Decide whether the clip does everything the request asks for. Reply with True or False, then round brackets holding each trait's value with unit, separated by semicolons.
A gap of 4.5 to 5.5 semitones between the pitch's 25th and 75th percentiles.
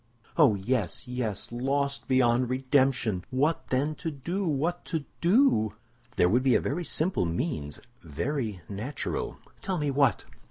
True (4.8 semitones)